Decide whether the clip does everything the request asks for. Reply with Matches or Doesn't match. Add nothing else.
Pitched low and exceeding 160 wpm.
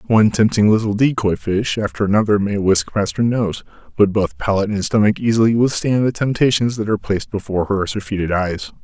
Matches